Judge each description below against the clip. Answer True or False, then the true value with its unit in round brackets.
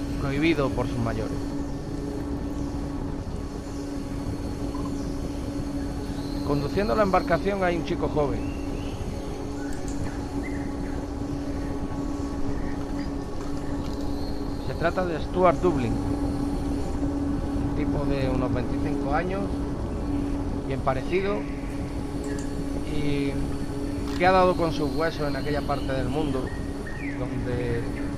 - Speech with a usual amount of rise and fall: False (7.2 semitones)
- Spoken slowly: True (80 wpm)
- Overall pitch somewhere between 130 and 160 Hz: True (135 Hz)